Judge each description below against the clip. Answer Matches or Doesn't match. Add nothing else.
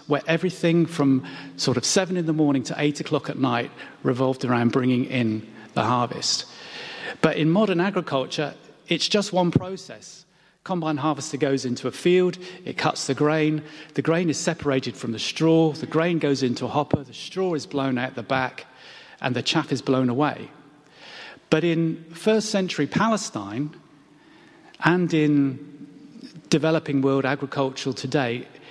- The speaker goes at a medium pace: Matches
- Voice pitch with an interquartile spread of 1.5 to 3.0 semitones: Doesn't match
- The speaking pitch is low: Doesn't match